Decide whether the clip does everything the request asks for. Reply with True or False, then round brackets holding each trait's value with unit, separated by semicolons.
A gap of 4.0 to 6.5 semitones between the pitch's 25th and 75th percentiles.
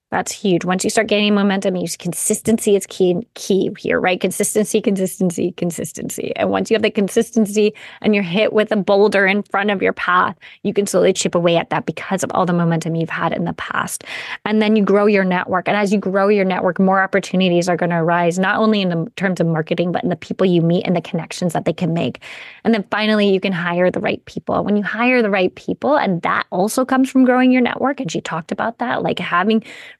False (3.0 semitones)